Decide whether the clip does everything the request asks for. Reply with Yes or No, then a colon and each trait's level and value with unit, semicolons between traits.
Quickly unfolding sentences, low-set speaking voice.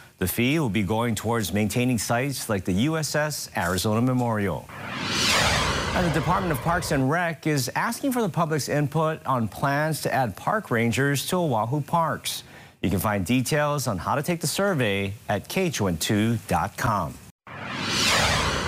No: average, 150 wpm; low, 130 Hz